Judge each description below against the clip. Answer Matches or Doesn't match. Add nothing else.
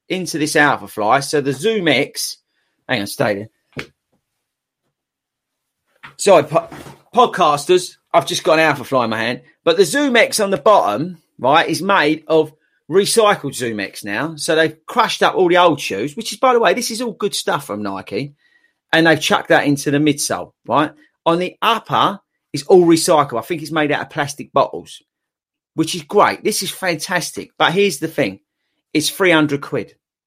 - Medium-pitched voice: Matches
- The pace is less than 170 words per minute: Doesn't match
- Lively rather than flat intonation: Doesn't match